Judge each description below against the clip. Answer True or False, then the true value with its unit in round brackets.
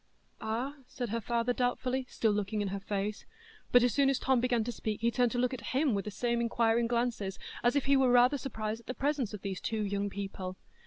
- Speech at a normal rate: False (235 wpm)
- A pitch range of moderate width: True (3.0 semitones)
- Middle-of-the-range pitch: False (235 Hz)